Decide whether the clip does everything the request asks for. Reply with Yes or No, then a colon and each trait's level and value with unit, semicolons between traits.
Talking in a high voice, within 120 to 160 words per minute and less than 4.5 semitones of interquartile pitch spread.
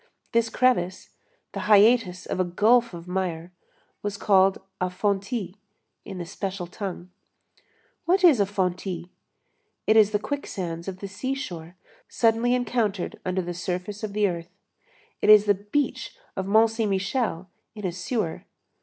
Yes: high, 200 Hz; average, 150 wpm; average, 3.5 semitones